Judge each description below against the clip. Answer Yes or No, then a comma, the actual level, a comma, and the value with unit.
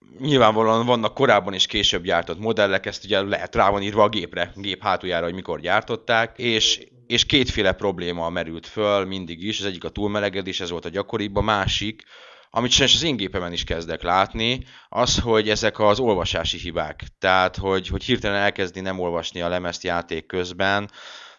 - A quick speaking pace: Yes, fast, 180 wpm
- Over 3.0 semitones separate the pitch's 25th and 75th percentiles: Yes, average, 3.4 semitones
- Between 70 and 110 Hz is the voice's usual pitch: Yes, low, 100 Hz